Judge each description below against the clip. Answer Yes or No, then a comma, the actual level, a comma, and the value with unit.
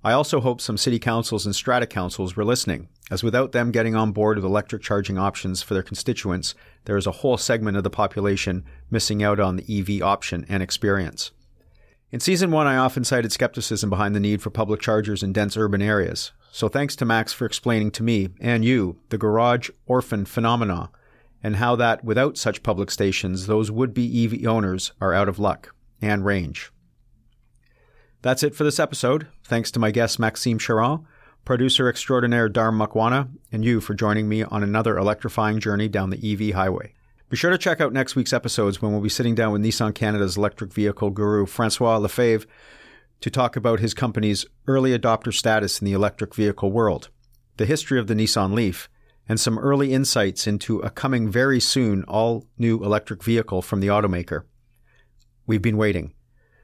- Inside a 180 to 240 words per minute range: Yes, average, 185 wpm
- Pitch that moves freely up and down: No, average, 2.8 semitones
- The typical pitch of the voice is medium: No, low, 110 Hz